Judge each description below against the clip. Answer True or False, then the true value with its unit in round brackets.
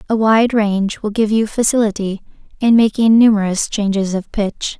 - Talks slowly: False (165 wpm)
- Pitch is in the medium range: False (215 Hz)